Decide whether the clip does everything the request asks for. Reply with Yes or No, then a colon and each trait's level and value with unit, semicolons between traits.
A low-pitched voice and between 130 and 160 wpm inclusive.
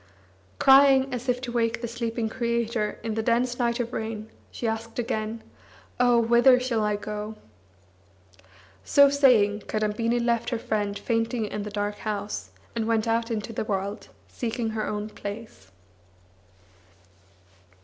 No: high, 230 Hz; average, 145 wpm